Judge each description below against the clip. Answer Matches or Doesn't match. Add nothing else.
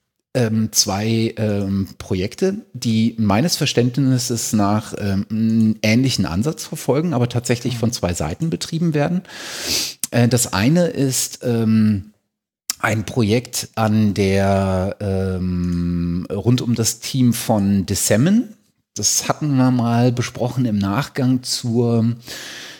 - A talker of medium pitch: Doesn't match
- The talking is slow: Matches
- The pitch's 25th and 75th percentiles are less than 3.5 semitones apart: Doesn't match